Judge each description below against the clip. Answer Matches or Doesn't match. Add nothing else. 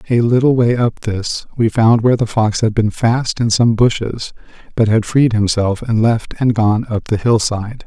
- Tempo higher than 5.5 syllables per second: Doesn't match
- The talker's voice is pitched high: Doesn't match